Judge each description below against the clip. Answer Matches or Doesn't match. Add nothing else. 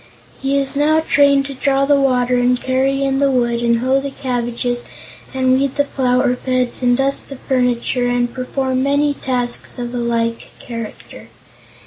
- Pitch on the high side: Matches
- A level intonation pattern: Matches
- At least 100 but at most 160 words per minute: Doesn't match